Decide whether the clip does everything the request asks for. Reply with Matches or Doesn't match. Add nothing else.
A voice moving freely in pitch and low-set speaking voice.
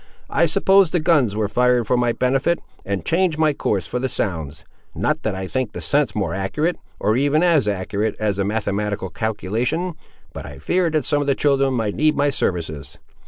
Matches